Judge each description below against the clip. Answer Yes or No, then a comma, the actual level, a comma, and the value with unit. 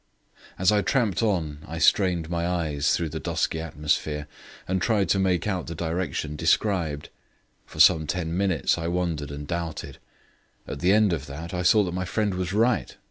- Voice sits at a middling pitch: No, very low, 85 Hz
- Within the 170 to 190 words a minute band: Yes, average, 185 wpm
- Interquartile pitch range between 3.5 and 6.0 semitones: No, average, 3.1 semitones